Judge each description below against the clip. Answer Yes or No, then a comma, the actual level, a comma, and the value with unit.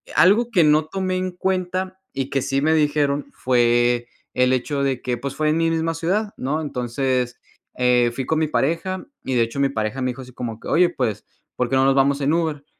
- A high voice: No, medium, 140 Hz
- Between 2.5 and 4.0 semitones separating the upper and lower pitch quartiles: No, average, 4.5 semitones